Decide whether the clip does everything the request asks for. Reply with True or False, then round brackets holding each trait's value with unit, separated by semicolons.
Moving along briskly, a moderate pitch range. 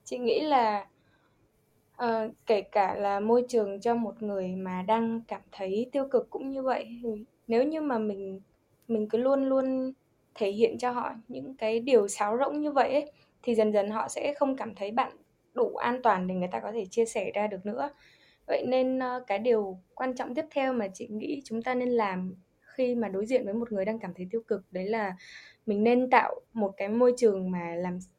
False (220 wpm; 4.0 semitones)